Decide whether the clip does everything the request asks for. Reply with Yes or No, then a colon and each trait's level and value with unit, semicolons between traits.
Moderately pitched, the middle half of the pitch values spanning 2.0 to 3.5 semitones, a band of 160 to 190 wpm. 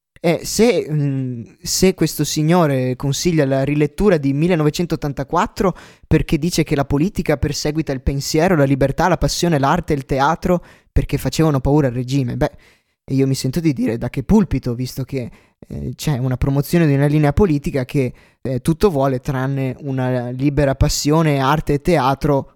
Yes: medium, 145 Hz; average, 3.2 semitones; average, 165 wpm